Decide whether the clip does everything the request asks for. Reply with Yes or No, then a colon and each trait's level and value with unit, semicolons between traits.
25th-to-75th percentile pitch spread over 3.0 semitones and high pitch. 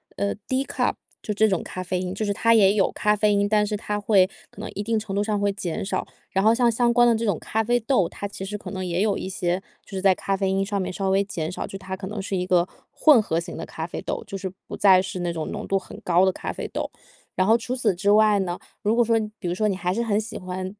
No: narrow, 2.5 semitones; high, 200 Hz